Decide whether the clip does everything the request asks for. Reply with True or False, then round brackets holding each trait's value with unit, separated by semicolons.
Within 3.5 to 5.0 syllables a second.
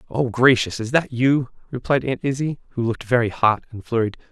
False (5.6 syllables/s)